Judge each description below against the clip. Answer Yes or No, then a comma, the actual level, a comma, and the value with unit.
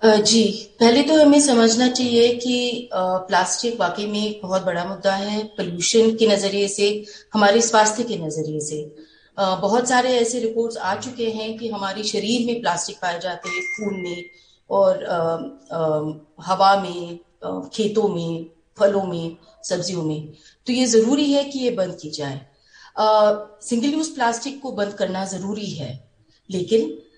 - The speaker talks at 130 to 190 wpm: Yes, average, 155 wpm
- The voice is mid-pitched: No, high, 200 Hz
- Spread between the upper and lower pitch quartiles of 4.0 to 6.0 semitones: Yes, average, 4.4 semitones